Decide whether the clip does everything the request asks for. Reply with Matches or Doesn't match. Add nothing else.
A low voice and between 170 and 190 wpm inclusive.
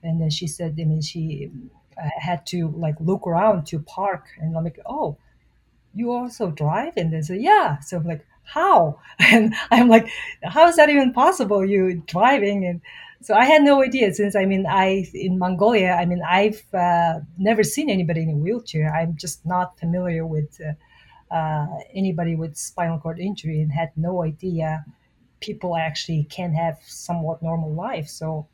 Doesn't match